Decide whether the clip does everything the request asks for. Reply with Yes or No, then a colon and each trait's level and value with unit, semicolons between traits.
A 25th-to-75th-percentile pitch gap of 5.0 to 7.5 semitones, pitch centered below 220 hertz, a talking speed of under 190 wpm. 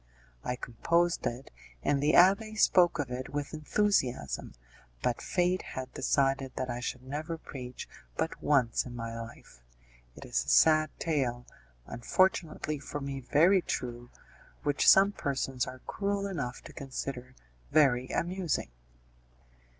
Yes: average, 5.3 semitones; medium, 140 Hz; slow, 135 wpm